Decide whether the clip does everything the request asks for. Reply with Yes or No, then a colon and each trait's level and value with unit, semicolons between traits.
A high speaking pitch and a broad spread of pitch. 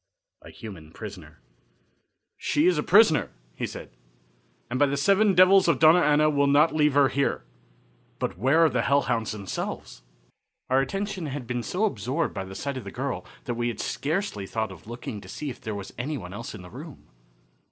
No: low, 135 Hz; wide, 6.3 semitones